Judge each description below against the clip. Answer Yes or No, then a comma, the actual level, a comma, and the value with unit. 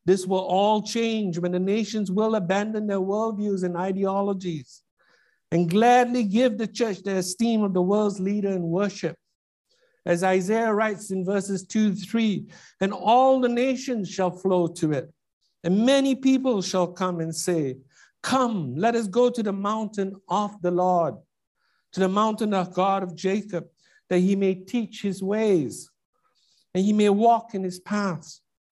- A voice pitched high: Yes, high, 195 Hz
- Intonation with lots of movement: No, average, 3.2 semitones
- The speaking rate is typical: Yes, average, 165 wpm